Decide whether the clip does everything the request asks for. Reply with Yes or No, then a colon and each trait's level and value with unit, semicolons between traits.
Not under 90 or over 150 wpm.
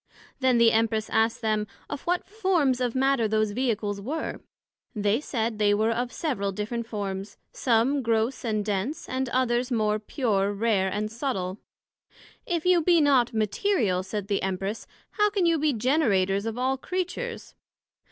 No: average, 160 wpm